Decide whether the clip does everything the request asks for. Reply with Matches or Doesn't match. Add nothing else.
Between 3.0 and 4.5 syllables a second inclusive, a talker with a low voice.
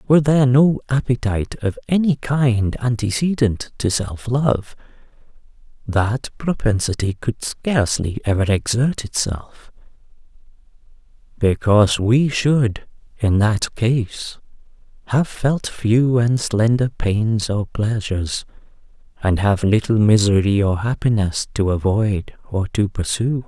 Matches